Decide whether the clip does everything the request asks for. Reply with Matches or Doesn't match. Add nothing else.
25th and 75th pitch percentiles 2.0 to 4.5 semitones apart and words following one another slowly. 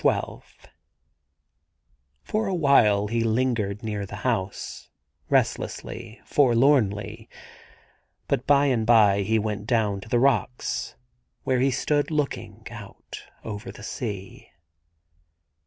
Matches